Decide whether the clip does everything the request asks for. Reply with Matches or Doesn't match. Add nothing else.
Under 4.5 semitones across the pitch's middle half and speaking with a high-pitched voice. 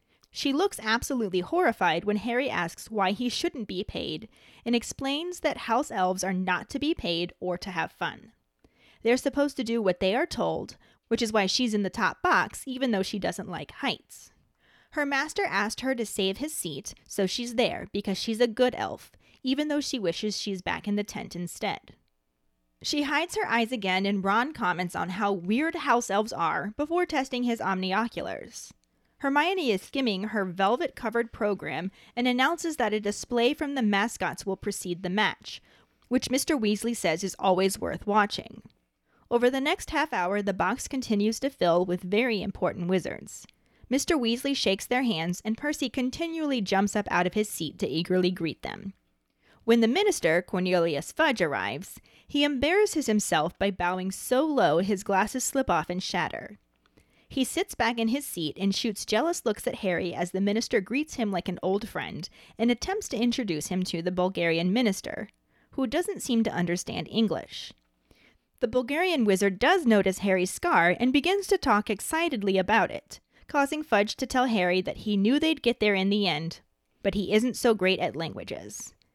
Doesn't match